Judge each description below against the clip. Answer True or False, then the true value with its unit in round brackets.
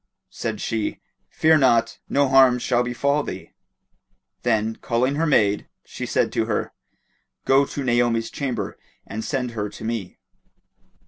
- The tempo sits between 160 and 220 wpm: False (140 wpm)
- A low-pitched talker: True (120 Hz)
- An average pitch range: True (3.1 semitones)